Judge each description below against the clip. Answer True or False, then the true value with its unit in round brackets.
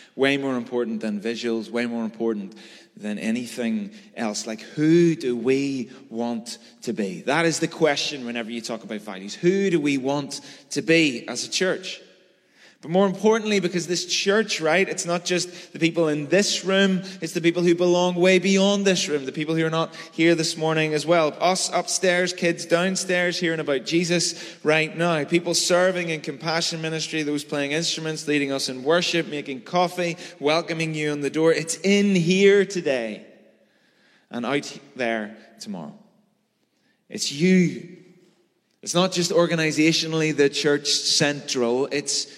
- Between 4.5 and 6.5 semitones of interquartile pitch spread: False (3.8 semitones)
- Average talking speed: True (165 wpm)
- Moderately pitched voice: True (165 Hz)